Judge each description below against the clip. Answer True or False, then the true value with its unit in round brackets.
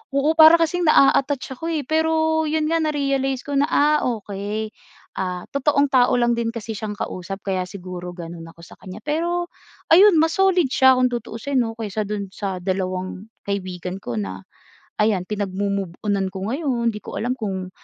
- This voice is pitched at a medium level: False (225 Hz)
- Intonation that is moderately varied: False (7.2 semitones)